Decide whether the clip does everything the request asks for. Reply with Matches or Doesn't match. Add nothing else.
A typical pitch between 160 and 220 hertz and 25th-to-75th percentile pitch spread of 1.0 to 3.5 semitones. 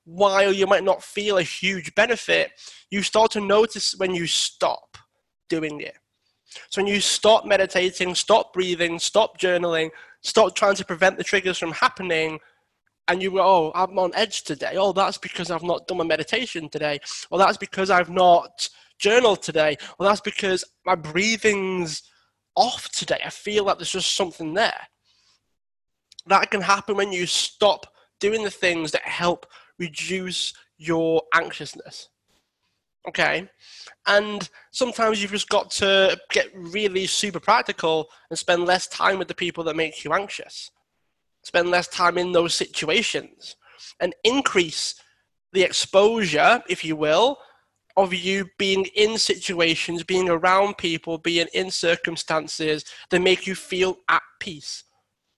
Matches